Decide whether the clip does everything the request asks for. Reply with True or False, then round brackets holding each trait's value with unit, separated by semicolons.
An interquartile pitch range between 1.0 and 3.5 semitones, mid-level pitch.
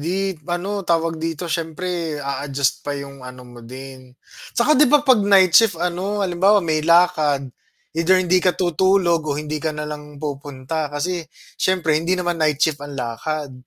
False (3.9 semitones; 160 Hz)